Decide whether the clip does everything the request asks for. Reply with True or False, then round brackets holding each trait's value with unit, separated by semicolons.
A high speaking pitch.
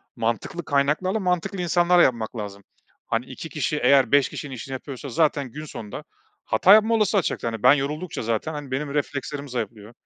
False (140 Hz)